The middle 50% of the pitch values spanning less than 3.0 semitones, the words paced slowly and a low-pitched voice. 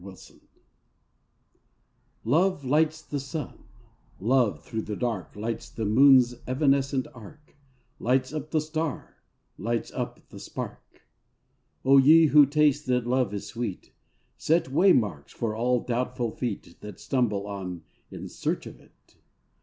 No: average, 4.6 semitones; slow, 130 wpm; low, 130 Hz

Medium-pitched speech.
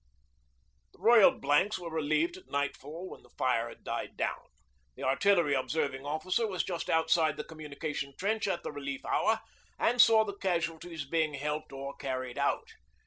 Yes: medium, 155 Hz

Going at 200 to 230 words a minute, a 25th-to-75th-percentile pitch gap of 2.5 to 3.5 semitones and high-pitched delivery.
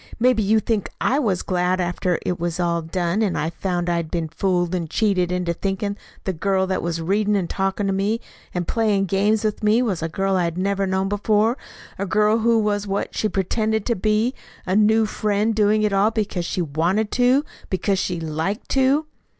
Yes: fast, 205 wpm; average, 3.2 semitones; high, 195 Hz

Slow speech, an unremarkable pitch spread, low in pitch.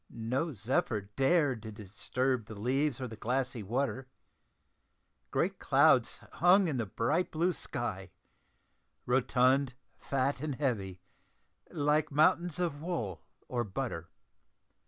Yes: slow, 115 wpm; average, 4.9 semitones; low, 130 Hz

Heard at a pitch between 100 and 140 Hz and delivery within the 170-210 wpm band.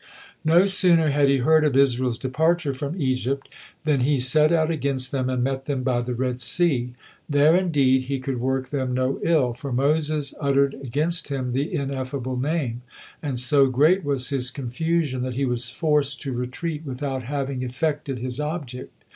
Yes: low, 135 Hz; average, 175 wpm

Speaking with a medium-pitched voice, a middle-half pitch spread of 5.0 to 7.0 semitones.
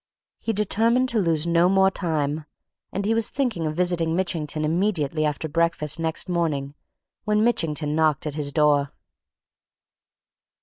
No: medium, 165 Hz; average, 4.0 semitones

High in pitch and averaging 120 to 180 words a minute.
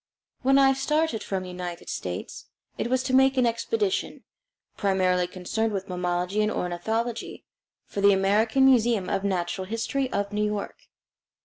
Yes: high, 210 Hz; average, 150 wpm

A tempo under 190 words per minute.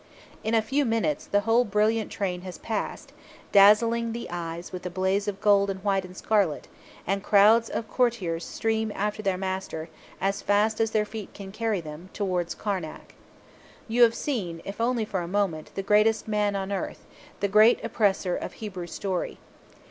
Yes: average, 180 wpm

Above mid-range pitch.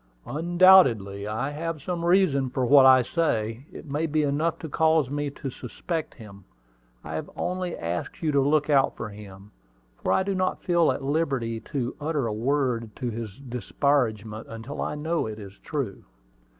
No: medium, 140 Hz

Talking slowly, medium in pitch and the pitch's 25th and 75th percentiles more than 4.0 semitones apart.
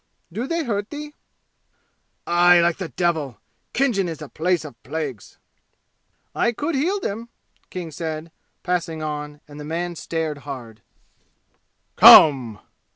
Yes: slow, 130 wpm; medium, 165 Hz; average, 5.1 semitones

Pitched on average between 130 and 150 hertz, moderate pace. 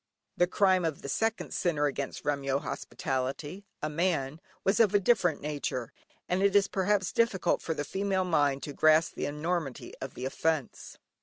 No: medium, 160 Hz; average, 170 wpm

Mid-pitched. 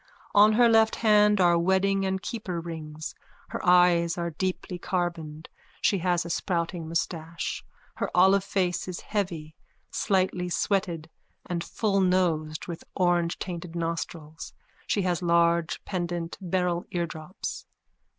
Yes: medium, 175 Hz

